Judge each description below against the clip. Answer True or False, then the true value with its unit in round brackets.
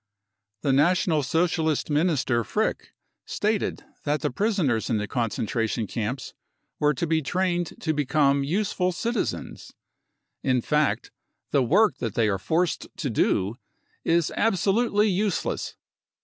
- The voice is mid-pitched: True (155 Hz)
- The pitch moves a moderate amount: False (6.3 semitones)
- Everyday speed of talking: False (125 wpm)